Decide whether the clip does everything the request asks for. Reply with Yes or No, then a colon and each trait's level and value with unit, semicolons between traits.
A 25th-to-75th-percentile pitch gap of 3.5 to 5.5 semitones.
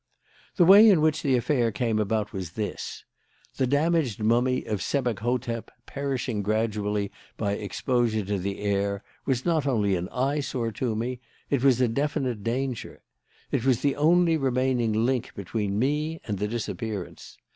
Yes: average, 4.4 semitones